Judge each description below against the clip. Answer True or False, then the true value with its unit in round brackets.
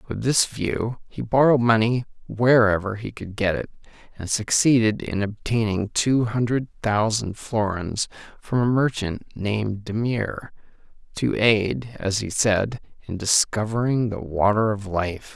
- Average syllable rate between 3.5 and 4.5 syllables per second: True (4.2 syllables/s)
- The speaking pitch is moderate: False (110 Hz)